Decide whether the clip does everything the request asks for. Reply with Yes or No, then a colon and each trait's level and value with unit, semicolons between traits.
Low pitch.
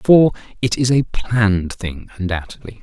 Yes: low, 110 Hz